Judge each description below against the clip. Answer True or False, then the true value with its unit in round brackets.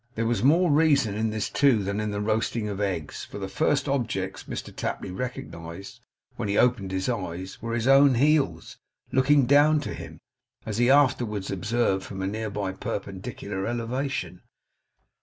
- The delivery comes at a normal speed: True (165 wpm)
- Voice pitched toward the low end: True (110 Hz)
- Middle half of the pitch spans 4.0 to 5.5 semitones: True (5.2 semitones)